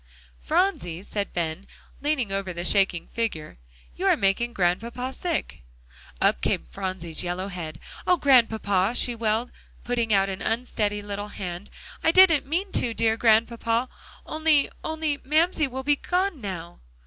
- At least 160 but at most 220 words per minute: No, average, 145 wpm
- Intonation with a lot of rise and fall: Yes, wide, 6.3 semitones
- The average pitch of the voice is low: No, high, 225 Hz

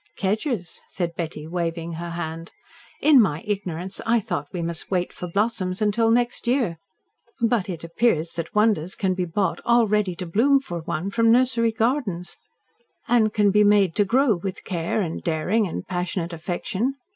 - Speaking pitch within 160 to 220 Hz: Yes, high, 190 Hz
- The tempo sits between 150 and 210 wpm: Yes, average, 170 wpm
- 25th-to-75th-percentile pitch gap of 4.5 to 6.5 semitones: Yes, average, 4.9 semitones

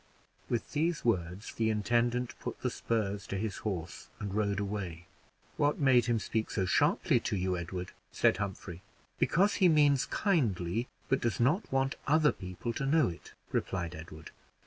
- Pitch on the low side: Yes, low, 110 Hz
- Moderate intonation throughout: No, wide, 6.2 semitones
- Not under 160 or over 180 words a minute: Yes, average, 165 wpm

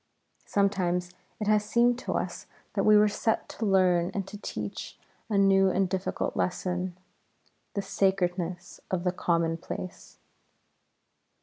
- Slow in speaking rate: Yes, slow, 130 wpm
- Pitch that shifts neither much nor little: No, narrow, 2.3 semitones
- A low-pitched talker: No, high, 190 Hz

